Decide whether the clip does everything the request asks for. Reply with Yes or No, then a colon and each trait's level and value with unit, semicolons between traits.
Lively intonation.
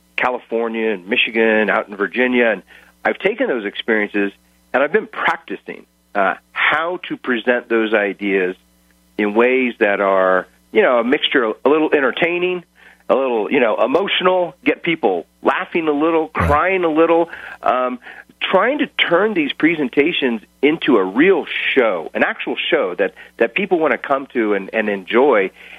Yes: wide, 8.4 semitones